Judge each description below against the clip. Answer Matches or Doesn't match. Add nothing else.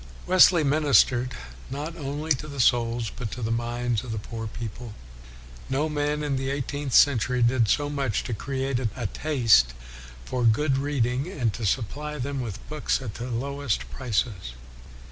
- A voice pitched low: Matches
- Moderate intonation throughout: Matches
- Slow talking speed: Doesn't match